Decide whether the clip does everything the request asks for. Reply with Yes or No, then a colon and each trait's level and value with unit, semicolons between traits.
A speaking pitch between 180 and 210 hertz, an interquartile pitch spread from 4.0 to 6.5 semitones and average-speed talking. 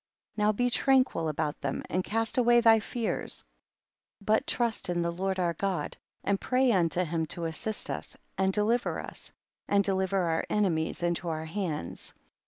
Yes: high, 190 Hz; average, 4.6 semitones; average, 175 wpm